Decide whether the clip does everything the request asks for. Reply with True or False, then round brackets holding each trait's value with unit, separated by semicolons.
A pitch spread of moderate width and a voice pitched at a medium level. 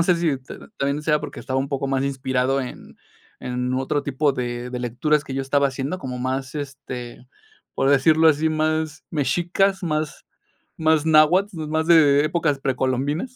True (3.0 semitones; 145 Hz)